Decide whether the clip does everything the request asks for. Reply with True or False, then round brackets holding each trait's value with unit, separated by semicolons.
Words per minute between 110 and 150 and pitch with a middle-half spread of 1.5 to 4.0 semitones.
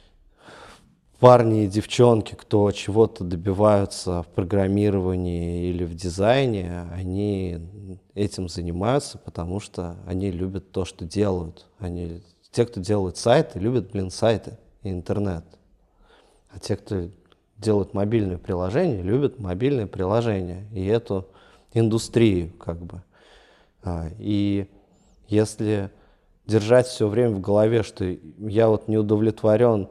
True (115 wpm; 3.2 semitones)